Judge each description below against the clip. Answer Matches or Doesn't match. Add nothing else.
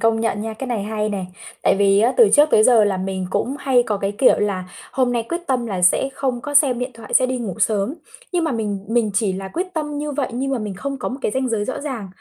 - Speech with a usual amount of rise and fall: Matches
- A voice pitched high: Matches